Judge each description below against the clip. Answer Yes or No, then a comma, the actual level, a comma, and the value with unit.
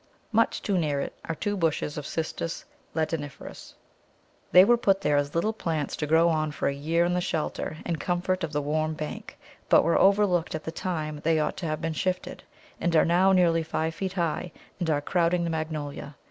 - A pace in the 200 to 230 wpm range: Yes, fast, 205 wpm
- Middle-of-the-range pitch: Yes, medium, 165 Hz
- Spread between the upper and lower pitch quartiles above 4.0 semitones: No, narrow, 2.6 semitones